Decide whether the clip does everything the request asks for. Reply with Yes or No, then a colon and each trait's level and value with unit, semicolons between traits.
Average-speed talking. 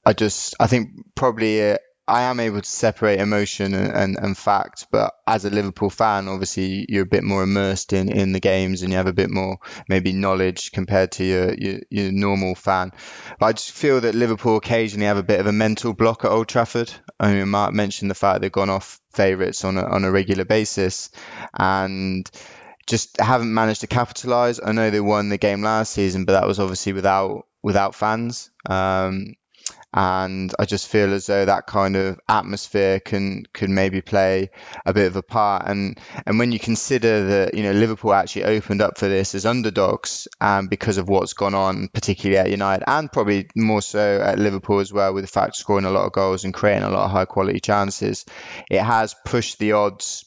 No: fast, 210 wpm